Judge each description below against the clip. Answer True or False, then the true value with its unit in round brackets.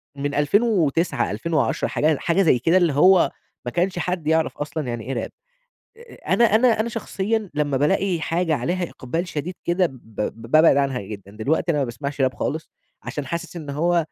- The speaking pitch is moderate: True (160 Hz)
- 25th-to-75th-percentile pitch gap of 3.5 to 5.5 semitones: True (4.3 semitones)